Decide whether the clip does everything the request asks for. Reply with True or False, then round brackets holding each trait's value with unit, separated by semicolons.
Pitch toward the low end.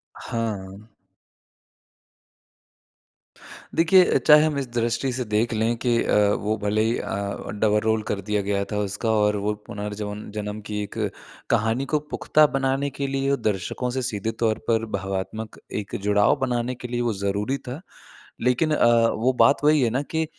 True (115 Hz)